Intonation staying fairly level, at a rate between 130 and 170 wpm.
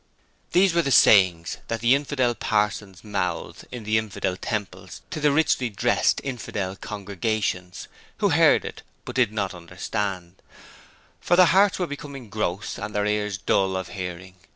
No: average, 5.1 semitones; average, 155 wpm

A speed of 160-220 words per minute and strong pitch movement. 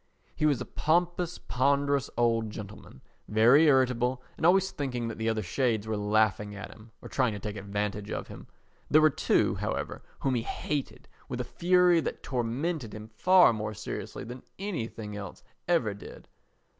Yes: average, 170 wpm; wide, 5.7 semitones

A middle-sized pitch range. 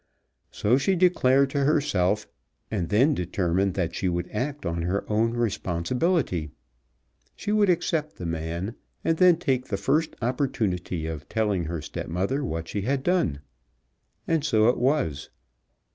No: wide, 8.5 semitones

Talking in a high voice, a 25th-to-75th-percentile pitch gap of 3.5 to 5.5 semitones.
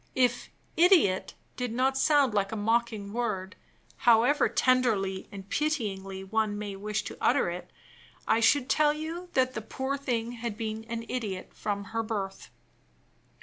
Yes: high, 225 Hz; average, 4.0 semitones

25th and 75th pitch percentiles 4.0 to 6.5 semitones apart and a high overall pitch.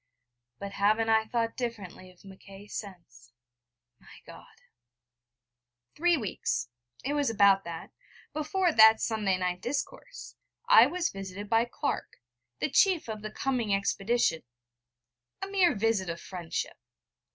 Yes: average, 5.0 semitones; high, 215 Hz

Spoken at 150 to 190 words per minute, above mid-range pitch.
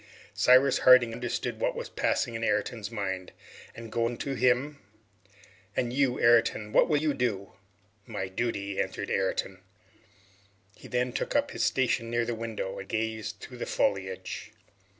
No: average, 160 wpm; low, 115 Hz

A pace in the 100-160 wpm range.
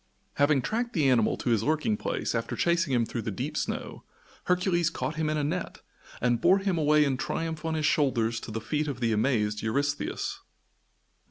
No: average, 195 wpm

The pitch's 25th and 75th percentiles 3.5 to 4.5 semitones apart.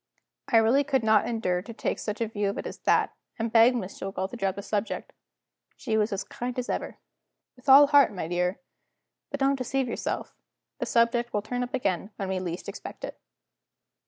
Yes: average, 4.0 semitones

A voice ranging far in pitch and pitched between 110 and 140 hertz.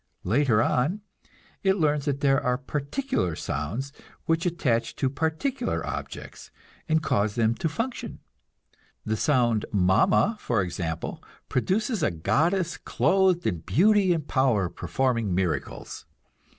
Yes: wide, 7.8 semitones; low, 135 Hz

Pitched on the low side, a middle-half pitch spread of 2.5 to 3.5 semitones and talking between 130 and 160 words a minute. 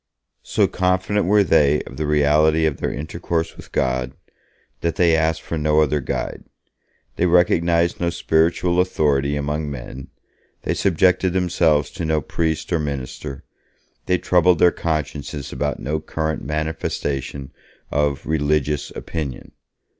Yes: very low, 80 Hz; average, 2.8 semitones; slow, 135 wpm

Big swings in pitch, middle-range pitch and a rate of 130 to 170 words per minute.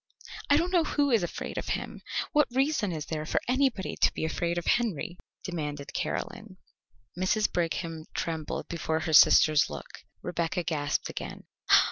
Yes: wide, 7.1 semitones; medium, 175 Hz; average, 155 wpm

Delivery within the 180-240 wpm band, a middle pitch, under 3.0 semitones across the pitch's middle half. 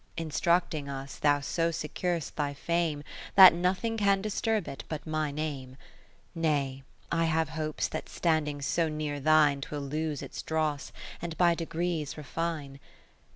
No: average, 150 wpm; medium, 155 Hz; narrow, 2.6 semitones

